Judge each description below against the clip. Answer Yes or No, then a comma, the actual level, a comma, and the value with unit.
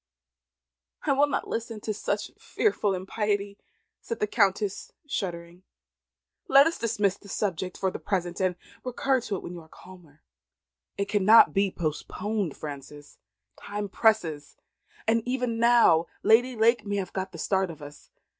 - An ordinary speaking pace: Yes, average, 155 wpm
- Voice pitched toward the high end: Yes, high, 200 Hz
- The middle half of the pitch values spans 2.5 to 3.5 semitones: No, average, 4.0 semitones